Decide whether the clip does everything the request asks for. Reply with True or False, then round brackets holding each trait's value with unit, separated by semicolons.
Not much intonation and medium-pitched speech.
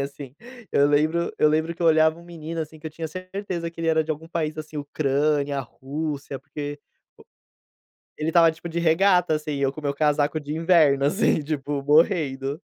True (2.3 semitones; 155 Hz)